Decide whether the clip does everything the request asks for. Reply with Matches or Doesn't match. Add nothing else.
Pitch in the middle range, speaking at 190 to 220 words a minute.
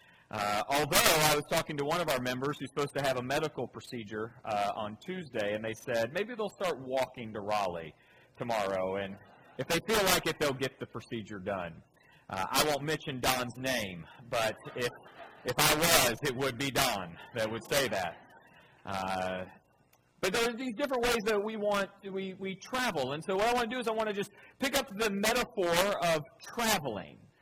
Matches